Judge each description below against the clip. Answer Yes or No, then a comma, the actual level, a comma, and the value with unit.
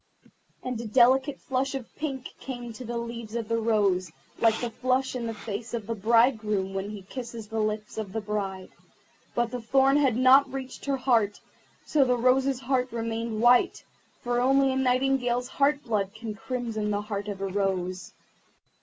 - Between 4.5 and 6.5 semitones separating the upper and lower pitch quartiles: No, average, 3.3 semitones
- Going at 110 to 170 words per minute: No, average, 185 wpm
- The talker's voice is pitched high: Yes, high, 235 Hz